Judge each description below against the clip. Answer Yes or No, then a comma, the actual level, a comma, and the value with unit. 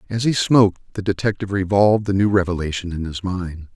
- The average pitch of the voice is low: Yes, very low, 95 Hz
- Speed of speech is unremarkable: Yes, average, 190 wpm